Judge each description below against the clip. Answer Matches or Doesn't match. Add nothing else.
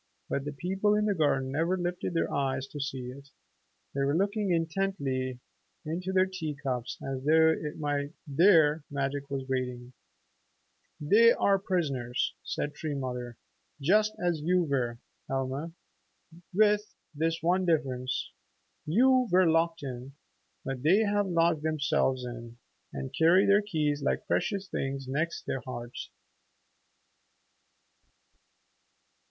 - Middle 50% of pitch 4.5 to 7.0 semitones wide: Matches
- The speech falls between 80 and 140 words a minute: Matches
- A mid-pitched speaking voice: Matches